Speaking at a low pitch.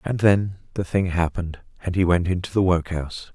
Yes: very low, 90 Hz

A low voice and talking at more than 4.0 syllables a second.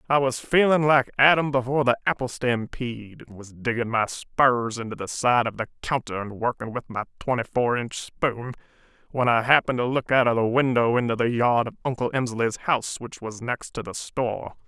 Yes: low, 120 Hz; 5.4 syllables/s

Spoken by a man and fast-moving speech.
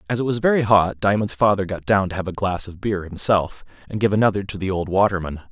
Yes: male; fast, 250 wpm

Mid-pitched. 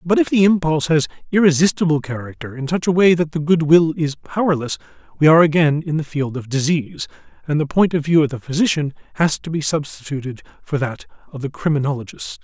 Yes: medium, 155 Hz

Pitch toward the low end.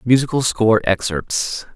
Yes: low, 115 Hz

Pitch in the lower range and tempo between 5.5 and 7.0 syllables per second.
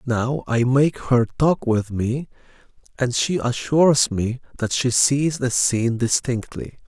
No: low, 125 Hz; 3.9 syllables/s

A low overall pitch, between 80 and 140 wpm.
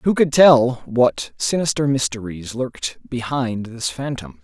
Yes: low, 125 Hz; slow, 135 wpm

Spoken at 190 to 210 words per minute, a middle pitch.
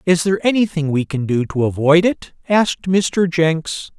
No: average, 180 wpm; medium, 165 Hz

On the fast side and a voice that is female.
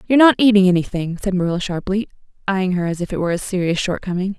Yes: fast, 220 wpm; female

